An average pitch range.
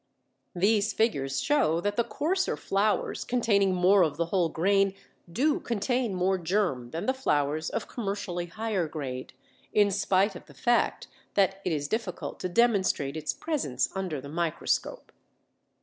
Yes: average, 5.0 semitones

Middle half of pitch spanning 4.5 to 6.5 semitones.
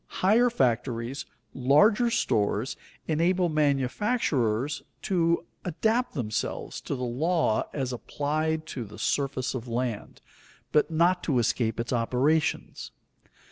Yes: wide, 5.5 semitones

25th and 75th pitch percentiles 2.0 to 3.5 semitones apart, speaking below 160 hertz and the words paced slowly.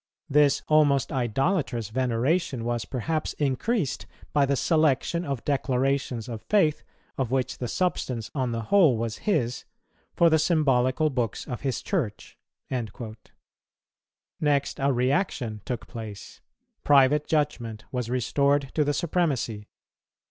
No: average, 3.9 semitones; low, 135 Hz; slow, 125 wpm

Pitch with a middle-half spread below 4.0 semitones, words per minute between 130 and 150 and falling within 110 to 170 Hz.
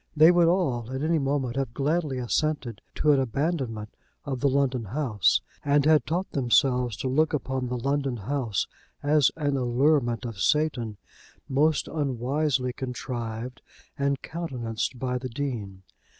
Yes: average, 3.4 semitones; average, 145 wpm; low, 135 Hz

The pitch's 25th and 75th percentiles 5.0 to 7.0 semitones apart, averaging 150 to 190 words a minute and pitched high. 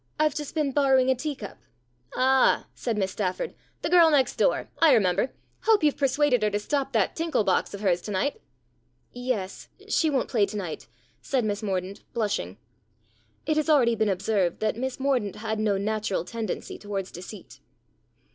Yes: wide, 5.5 semitones; average, 175 wpm; high, 230 Hz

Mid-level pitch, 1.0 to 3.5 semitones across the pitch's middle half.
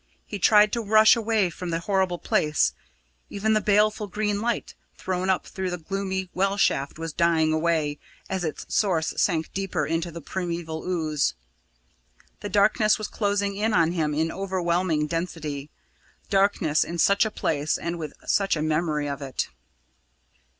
No: medium, 180 Hz; average, 4.0 semitones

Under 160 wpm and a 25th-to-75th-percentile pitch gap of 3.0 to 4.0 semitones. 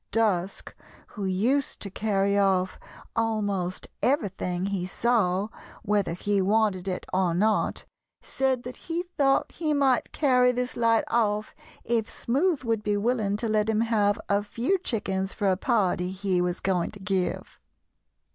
Yes: average, 150 wpm; average, 3.7 semitones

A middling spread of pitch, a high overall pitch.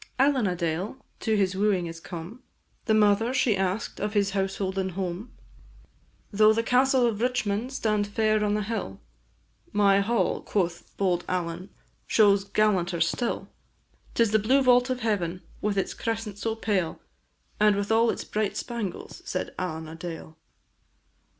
Yes: average, 3.4 semitones; high, 205 Hz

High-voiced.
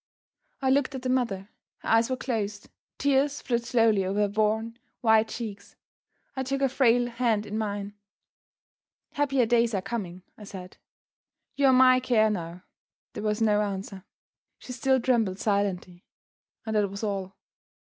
Yes: high, 220 Hz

